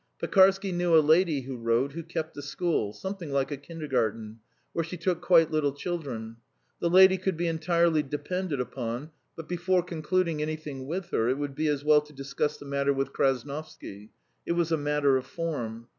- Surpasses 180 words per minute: Yes, average, 190 wpm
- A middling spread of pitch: Yes, average, 3.9 semitones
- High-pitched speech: No, medium, 150 Hz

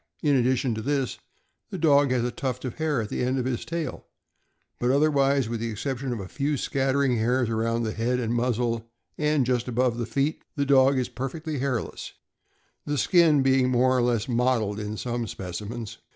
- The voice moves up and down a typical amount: Yes, average, 3.0 semitones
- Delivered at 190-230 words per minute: Yes, average, 195 wpm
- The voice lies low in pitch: Yes, low, 125 Hz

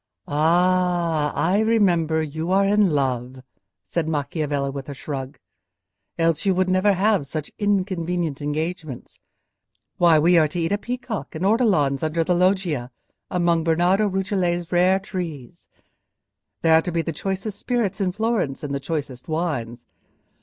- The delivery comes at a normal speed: Yes, average, 145 wpm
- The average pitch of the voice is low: No, medium, 170 Hz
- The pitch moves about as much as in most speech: Yes, average, 4.0 semitones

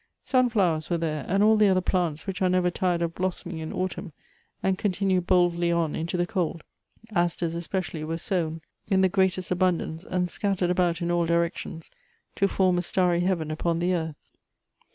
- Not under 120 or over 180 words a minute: No, average, 190 wpm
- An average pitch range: No, narrow, 1.9 semitones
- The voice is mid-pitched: Yes, medium, 175 Hz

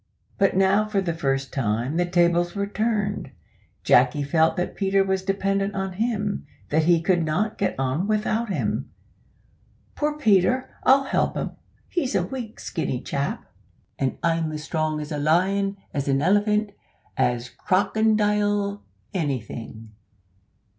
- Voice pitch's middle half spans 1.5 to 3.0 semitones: No, average, 5.0 semitones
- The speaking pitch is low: No, high, 190 Hz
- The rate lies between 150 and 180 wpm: No, average, 140 wpm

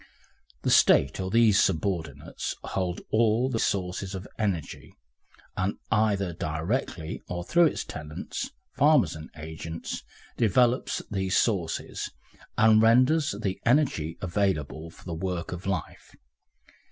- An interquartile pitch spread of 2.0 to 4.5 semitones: No, average, 5.2 semitones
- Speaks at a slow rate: Yes, slow, 120 wpm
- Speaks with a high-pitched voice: No, very low, 95 Hz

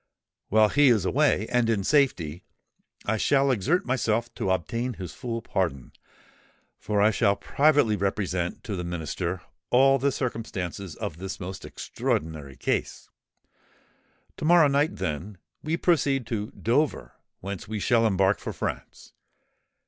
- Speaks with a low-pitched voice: Yes, low, 105 Hz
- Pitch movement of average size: No, wide, 5.8 semitones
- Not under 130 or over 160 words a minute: Yes, average, 140 wpm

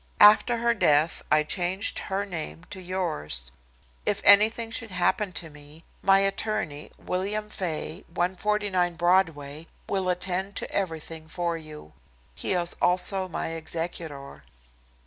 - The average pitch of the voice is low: No, medium, 180 Hz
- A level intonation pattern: No, average, 3.5 semitones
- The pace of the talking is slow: Yes, slow, 125 wpm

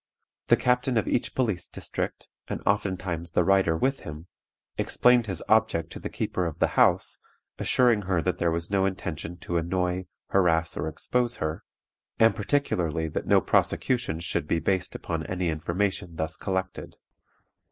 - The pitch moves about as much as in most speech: Yes, average, 3.7 semitones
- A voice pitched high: No, very low, 90 Hz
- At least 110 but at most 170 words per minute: Yes, average, 160 wpm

